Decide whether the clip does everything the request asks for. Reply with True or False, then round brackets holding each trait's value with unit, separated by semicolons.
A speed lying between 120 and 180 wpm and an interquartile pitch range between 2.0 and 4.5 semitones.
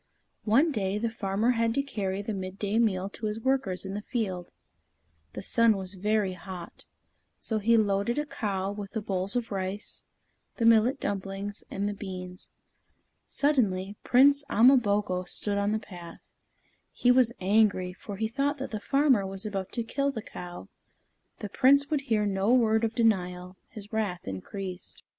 True (170 wpm; 3.3 semitones)